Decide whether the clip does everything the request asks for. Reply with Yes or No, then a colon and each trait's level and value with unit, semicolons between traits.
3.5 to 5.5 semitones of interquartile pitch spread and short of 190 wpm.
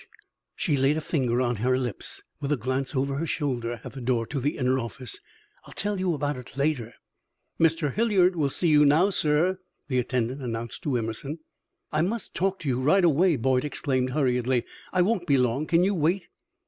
No: average, 4.5 semitones; average, 200 wpm